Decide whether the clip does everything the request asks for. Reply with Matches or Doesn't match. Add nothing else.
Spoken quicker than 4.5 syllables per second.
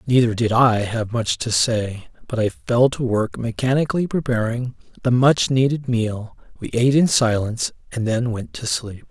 Matches